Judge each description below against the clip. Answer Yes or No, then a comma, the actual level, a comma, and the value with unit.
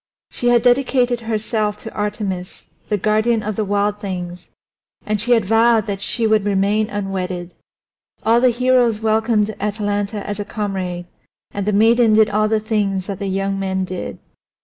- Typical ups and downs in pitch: No, narrow, 2.2 semitones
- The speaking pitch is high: Yes, high, 210 Hz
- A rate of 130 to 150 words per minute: No, average, 170 wpm